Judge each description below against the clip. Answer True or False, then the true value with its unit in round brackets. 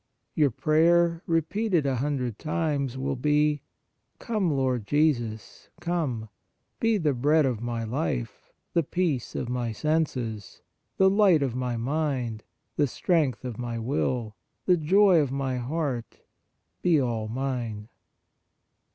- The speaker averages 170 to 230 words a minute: False (135 wpm)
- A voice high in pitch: False (140 Hz)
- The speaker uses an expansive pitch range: False (4.9 semitones)